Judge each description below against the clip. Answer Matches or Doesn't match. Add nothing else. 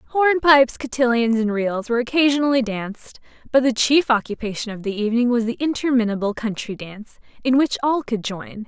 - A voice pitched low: Doesn't match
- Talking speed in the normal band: Matches